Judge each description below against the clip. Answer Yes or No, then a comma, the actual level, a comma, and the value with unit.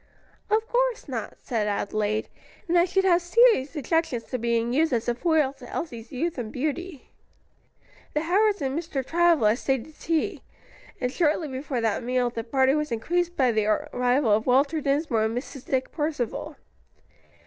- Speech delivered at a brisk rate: No, average, 170 wpm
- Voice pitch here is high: Yes, very high, 275 Hz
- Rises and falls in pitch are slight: No, wide, 5.6 semitones